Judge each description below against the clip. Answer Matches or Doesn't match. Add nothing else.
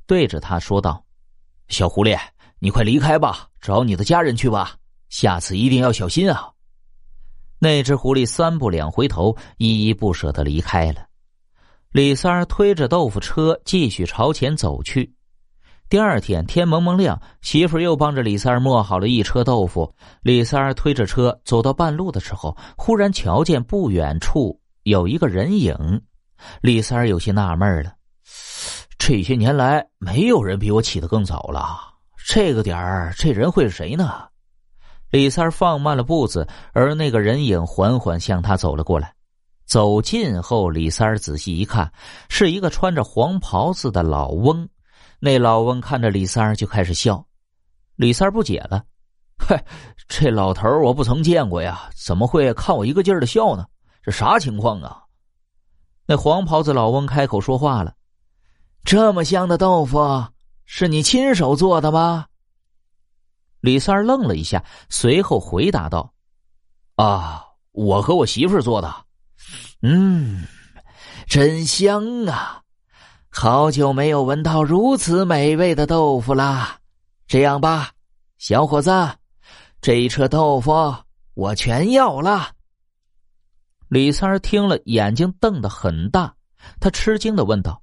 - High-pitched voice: Doesn't match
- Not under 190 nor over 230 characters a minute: Matches